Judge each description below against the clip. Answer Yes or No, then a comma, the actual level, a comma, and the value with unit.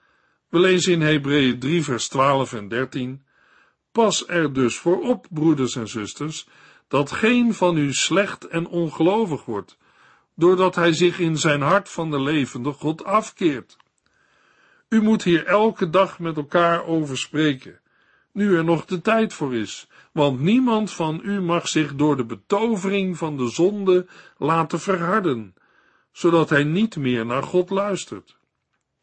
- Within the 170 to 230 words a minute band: No, average, 150 wpm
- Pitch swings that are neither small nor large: Yes, average, 4.6 semitones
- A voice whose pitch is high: No, medium, 165 Hz